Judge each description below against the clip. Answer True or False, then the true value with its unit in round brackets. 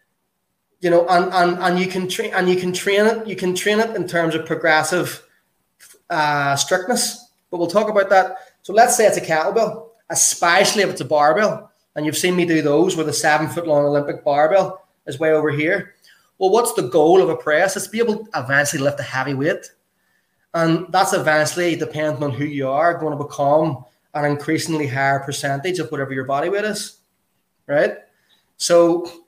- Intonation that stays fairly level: False (4.1 semitones)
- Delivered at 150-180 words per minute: False (195 wpm)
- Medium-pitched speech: True (170 Hz)